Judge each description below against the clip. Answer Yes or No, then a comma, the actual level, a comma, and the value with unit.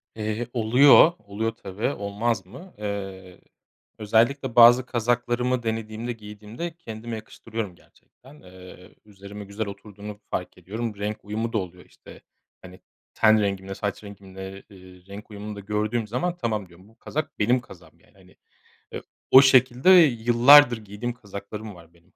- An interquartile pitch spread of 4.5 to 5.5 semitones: No, average, 3.1 semitones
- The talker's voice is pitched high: No, low, 110 Hz